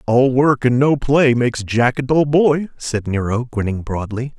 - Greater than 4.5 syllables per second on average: No, 4.4 syllables/s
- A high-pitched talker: No, low, 125 Hz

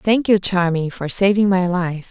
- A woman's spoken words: Yes, female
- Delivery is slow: No, average, 200 wpm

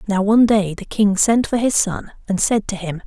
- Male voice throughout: No, female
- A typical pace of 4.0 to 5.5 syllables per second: Yes, 5.1 syllables/s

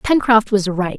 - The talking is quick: No, average, 180 wpm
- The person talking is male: No, female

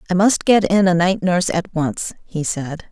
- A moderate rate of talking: No, fast, 225 wpm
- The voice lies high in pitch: No, medium, 180 Hz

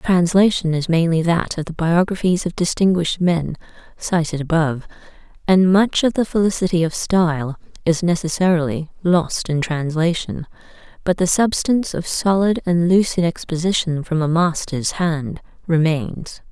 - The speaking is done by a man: No, female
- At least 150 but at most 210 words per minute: No, average, 140 wpm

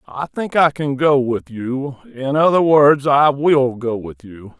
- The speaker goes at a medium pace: Yes, average, 195 wpm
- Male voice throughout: Yes, male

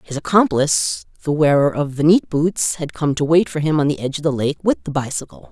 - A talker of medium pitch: Yes, medium, 155 Hz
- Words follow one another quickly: Yes, fast, 250 wpm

